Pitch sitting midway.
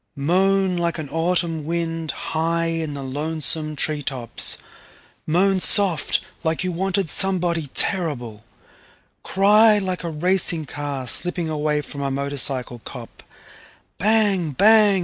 Yes: medium, 165 Hz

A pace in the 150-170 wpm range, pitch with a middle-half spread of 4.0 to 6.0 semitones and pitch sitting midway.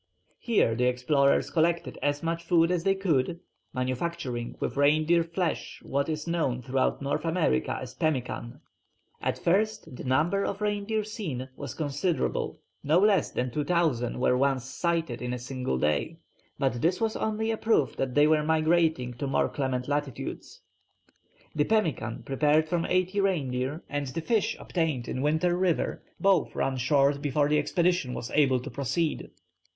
Yes: average, 160 wpm; average, 4.7 semitones; medium, 150 Hz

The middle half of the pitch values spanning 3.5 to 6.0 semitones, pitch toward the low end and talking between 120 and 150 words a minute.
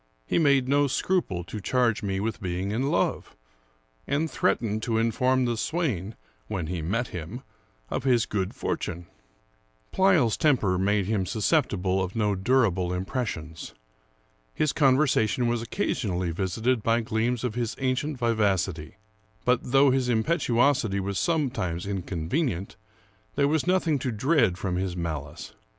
Yes: wide, 5.6 semitones; low, 115 Hz; average, 140 wpm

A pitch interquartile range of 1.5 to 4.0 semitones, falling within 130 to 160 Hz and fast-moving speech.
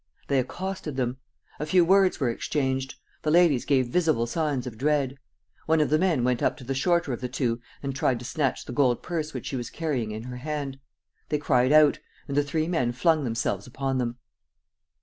Yes: average, 3.6 semitones; low, 135 Hz; fast, 210 wpm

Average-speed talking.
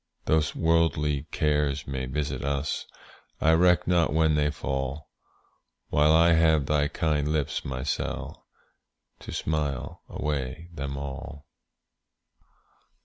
No: slow, 115 wpm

